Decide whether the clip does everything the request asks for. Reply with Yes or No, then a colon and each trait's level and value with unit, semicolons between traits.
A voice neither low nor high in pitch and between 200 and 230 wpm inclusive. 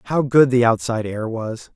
No: low, 120 Hz; fast, 205 wpm